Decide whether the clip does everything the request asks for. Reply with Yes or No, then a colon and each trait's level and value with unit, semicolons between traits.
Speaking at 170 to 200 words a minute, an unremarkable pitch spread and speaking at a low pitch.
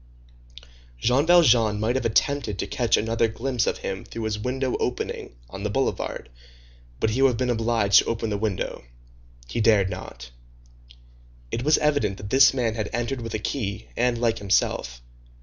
Yes: average, 175 wpm; average, 3.2 semitones; low, 115 Hz